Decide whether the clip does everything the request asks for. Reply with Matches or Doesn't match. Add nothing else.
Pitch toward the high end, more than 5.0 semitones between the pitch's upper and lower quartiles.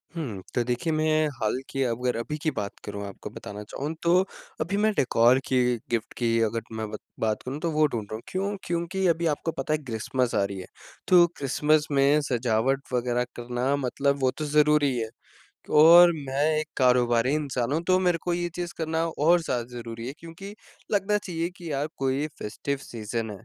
Doesn't match